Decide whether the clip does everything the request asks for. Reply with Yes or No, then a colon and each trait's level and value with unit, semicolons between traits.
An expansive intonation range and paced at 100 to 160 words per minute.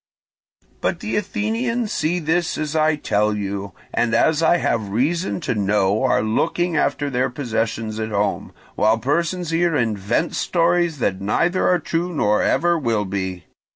Yes: wide, 8.3 semitones; average, 155 wpm